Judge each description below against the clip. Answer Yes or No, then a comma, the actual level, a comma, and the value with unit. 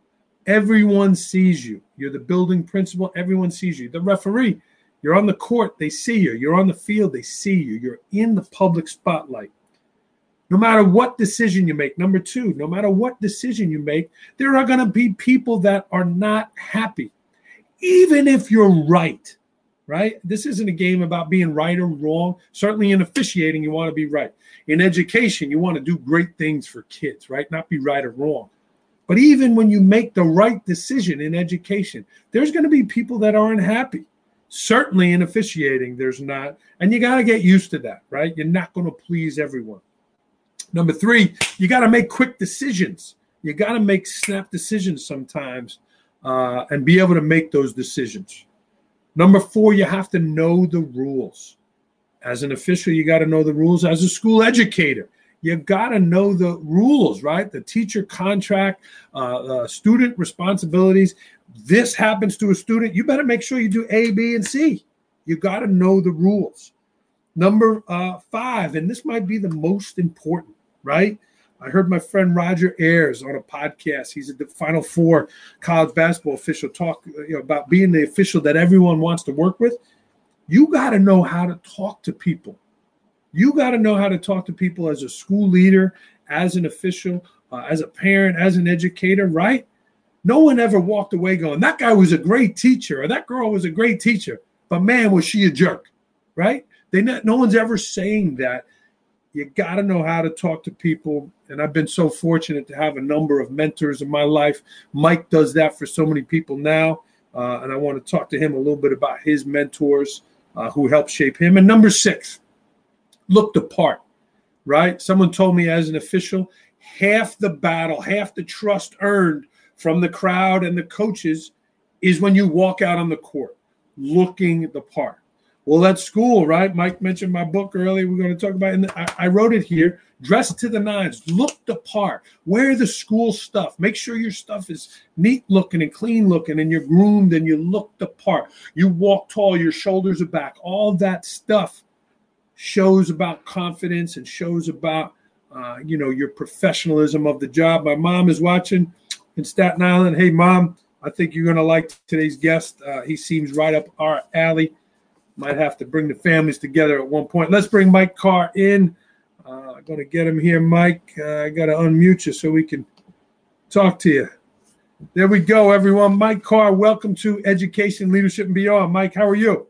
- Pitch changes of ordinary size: Yes, average, 4.5 semitones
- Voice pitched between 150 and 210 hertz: Yes, medium, 185 Hz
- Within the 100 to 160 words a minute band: No, average, 195 wpm